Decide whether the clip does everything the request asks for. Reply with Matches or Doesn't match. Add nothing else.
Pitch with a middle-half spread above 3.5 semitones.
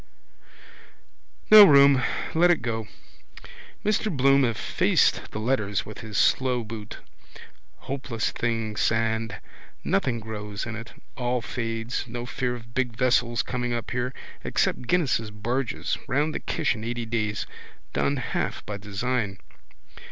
Doesn't match